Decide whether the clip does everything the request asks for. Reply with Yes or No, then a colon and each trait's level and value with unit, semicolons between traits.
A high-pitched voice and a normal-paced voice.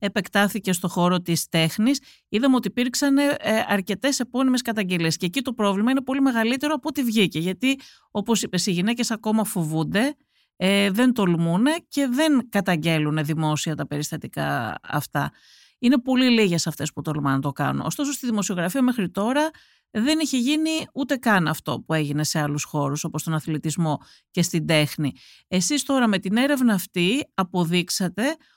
Yes: high, 205 Hz; average, 160 wpm